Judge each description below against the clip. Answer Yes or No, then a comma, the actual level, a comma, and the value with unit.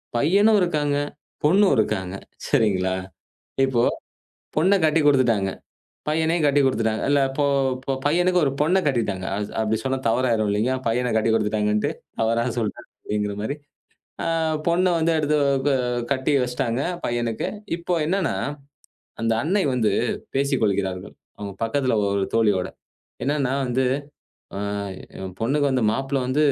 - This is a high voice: No, low, 130 Hz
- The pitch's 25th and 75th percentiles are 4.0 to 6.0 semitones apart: Yes, wide, 5.4 semitones